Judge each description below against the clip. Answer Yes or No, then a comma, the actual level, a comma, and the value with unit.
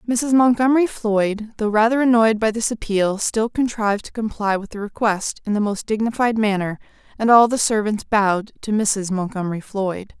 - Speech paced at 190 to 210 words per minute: No, average, 175 wpm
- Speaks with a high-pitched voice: Yes, high, 215 Hz